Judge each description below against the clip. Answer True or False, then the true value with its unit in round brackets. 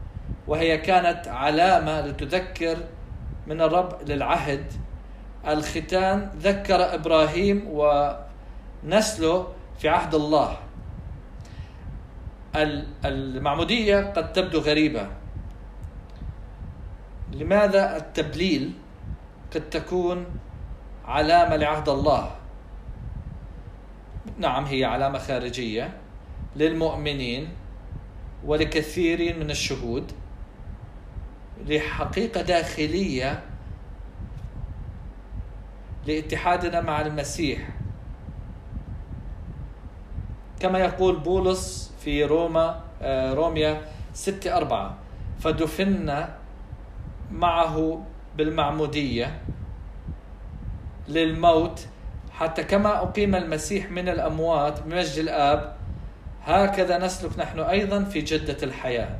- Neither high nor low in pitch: True (150 Hz)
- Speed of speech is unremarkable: False (65 wpm)